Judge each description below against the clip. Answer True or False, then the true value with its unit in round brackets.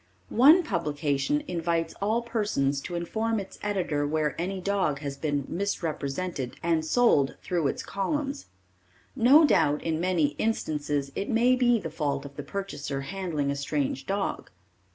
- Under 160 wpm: True (150 wpm)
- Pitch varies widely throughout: True (5.9 semitones)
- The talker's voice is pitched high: False (170 Hz)